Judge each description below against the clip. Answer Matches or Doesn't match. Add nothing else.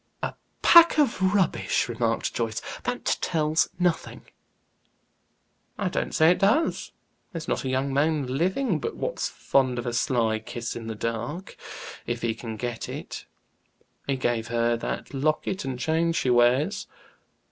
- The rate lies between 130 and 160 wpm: Matches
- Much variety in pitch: Matches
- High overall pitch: Doesn't match